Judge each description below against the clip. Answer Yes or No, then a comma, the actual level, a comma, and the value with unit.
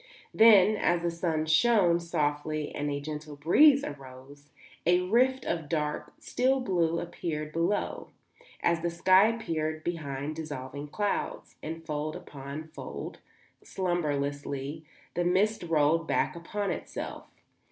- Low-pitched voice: No, medium, 165 Hz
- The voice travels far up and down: No, average, 3.4 semitones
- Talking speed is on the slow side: Yes, slow, 125 wpm